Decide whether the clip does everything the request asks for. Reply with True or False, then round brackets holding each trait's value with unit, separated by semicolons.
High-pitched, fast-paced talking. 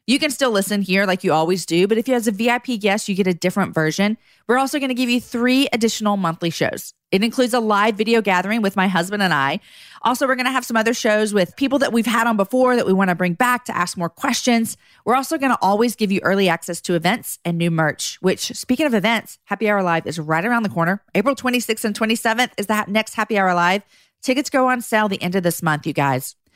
True (215 Hz; 250 wpm)